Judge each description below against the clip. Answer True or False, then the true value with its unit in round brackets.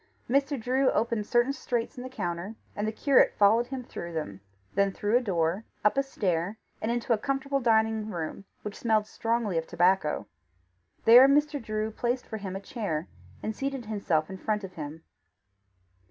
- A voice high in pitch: True (220 Hz)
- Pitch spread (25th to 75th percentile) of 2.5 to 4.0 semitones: False (4.4 semitones)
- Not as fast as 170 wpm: False (180 wpm)